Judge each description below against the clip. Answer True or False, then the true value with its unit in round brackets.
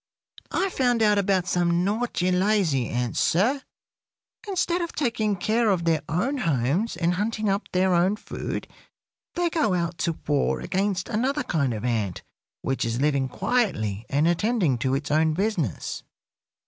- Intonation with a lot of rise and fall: True (6.7 semitones)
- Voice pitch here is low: False (180 Hz)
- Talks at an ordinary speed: True (155 wpm)